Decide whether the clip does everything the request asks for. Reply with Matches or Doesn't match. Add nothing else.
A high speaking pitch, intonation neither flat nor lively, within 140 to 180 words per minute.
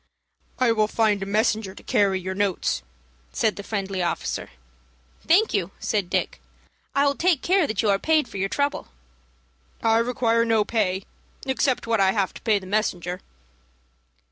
Matches